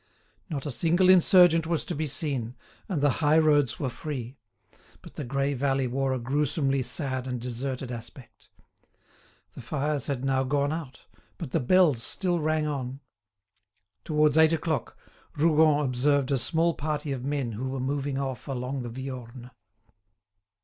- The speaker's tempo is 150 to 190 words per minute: Yes, average, 155 wpm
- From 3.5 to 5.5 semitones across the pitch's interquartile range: No, average, 3.0 semitones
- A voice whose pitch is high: No, medium, 140 Hz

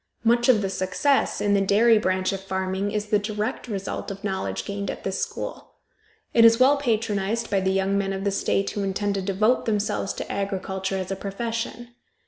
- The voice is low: No, high, 200 Hz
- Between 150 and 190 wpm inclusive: No, average, 200 wpm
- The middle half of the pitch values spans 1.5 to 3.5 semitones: Yes, narrow, 2.5 semitones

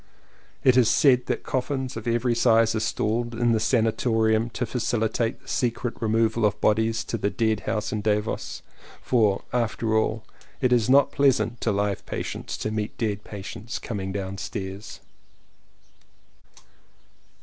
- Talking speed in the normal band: Yes, average, 150 wpm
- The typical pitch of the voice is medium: No, low, 110 Hz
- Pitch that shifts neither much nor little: No, narrow, 2.0 semitones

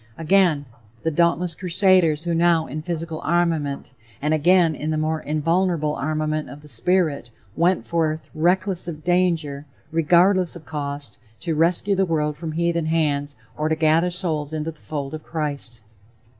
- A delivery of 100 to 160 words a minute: Yes, average, 155 wpm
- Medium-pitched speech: Yes, medium, 160 Hz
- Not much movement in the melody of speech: Yes, narrow, 2.3 semitones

